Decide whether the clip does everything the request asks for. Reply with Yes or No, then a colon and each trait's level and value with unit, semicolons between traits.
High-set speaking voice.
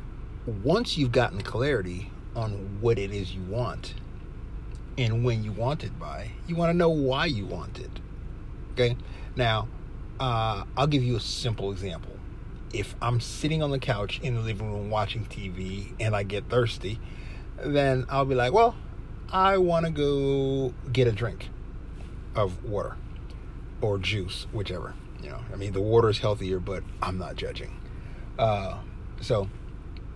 No: low, 110 Hz